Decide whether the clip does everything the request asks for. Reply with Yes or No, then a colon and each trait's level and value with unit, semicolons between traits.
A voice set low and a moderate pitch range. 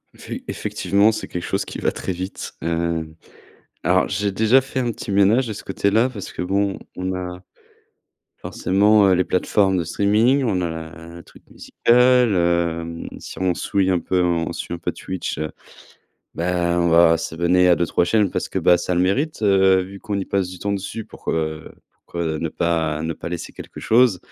Yes: very low, 90 Hz; average, 3.0 semitones